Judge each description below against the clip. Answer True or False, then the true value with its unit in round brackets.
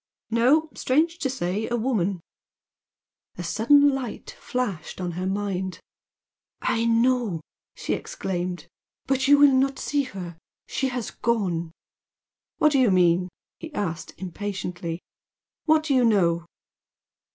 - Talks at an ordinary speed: False (130 wpm)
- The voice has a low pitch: False (220 Hz)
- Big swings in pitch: True (6.8 semitones)